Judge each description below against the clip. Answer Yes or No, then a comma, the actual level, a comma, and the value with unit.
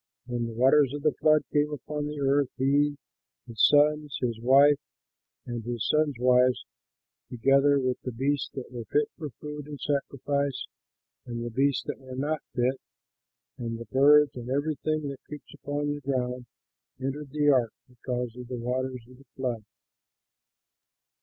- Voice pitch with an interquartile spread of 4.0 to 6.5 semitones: No, average, 2.8 semitones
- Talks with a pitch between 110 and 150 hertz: Yes, low, 135 Hz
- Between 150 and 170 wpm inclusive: Yes, average, 160 wpm